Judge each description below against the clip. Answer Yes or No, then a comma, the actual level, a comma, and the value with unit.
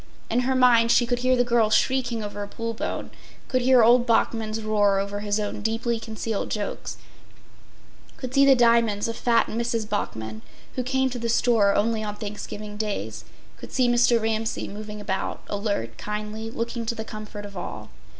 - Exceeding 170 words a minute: Yes, average, 180 wpm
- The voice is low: No, high, 225 Hz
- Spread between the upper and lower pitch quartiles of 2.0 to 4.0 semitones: Yes, narrow, 2.4 semitones